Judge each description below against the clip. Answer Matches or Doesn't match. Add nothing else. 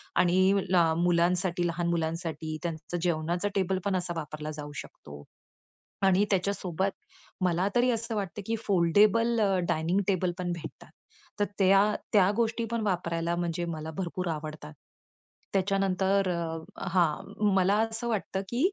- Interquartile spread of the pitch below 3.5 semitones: Matches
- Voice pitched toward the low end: Doesn't match